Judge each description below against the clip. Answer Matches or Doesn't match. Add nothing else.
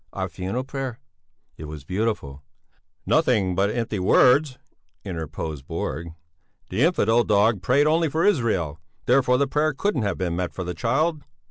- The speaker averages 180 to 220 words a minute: Doesn't match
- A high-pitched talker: Doesn't match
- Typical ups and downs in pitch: Doesn't match